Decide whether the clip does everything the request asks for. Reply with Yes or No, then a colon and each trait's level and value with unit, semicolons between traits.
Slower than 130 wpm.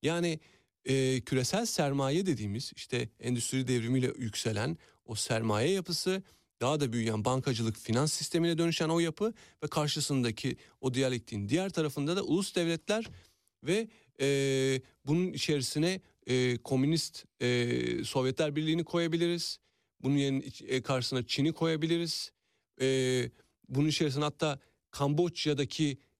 Yes: average, 115 wpm